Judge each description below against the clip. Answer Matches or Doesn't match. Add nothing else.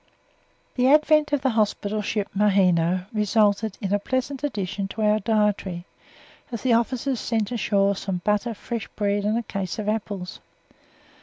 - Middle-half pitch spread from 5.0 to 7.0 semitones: Doesn't match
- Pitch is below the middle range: Doesn't match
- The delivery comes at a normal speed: Matches